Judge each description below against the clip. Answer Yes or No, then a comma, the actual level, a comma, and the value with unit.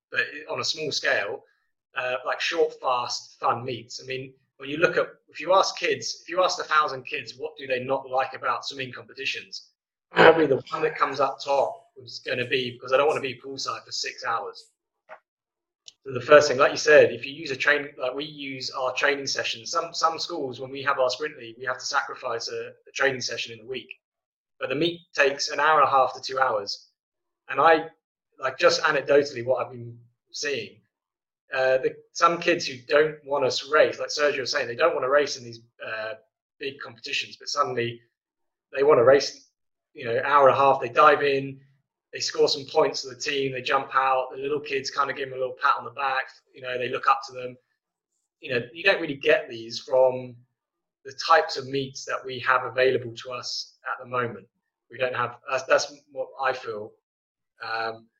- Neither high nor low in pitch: Yes, medium, 145 Hz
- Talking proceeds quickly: Yes, fast, 220 wpm